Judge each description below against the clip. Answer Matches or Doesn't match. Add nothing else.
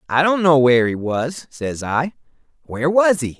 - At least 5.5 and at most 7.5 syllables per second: Doesn't match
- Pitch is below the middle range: Doesn't match